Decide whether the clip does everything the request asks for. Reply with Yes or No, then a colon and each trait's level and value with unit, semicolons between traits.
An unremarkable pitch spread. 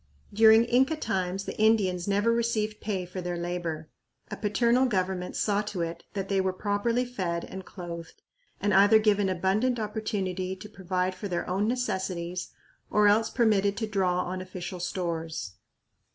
Yes: average, 3.0 semitones